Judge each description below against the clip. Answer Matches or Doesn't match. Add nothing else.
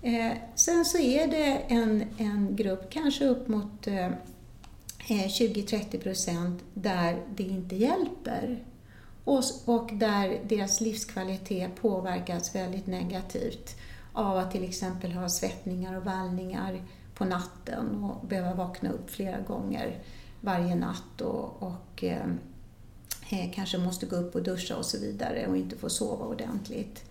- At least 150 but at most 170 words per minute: Doesn't match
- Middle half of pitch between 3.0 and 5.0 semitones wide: Matches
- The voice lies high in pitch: Matches